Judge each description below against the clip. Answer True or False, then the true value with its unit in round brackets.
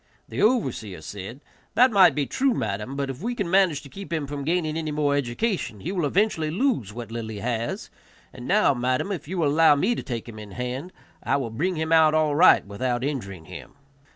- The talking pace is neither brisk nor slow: False (220 wpm)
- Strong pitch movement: True (6.6 semitones)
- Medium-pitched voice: True (145 Hz)